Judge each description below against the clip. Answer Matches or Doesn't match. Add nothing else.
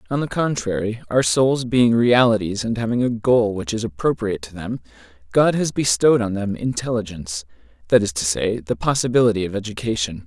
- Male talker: Matches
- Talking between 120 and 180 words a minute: Matches